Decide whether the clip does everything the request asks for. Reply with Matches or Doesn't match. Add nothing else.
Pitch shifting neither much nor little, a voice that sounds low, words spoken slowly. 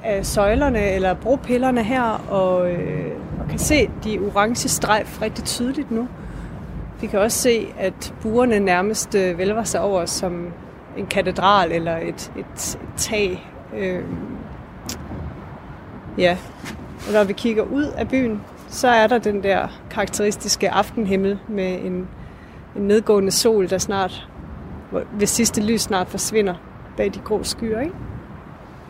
Doesn't match